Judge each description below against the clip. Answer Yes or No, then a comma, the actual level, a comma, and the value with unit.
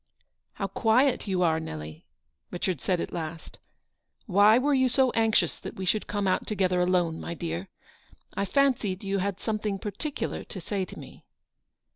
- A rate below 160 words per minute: No, average, 175 wpm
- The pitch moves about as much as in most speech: Yes, average, 3.7 semitones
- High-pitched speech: Yes, high, 195 Hz